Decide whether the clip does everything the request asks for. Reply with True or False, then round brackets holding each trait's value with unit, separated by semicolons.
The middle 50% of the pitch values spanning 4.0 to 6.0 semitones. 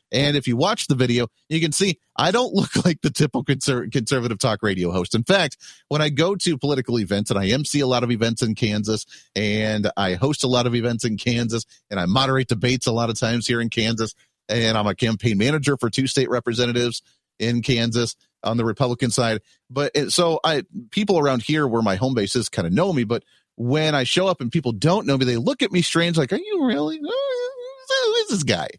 True (5.1 semitones)